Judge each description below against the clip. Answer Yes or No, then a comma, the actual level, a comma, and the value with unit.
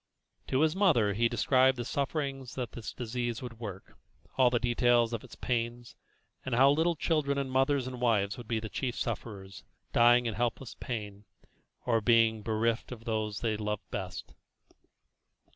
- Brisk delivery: No, average, 165 wpm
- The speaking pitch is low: Yes, low, 120 Hz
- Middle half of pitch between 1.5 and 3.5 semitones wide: Yes, average, 2.8 semitones